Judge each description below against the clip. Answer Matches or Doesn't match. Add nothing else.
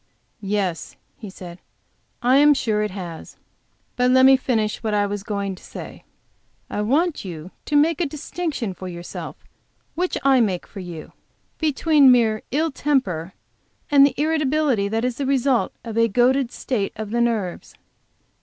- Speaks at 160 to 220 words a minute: Matches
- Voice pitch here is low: Doesn't match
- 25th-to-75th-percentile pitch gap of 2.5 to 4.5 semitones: Doesn't match